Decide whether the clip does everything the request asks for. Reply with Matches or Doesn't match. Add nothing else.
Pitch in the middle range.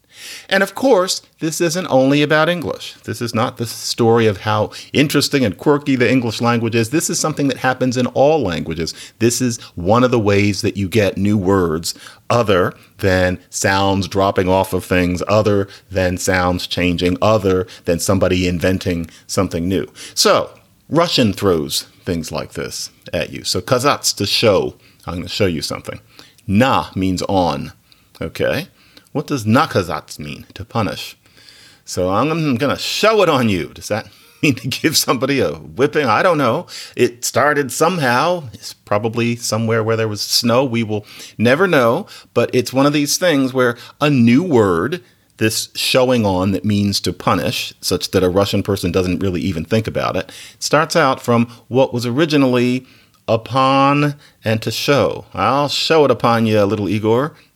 Doesn't match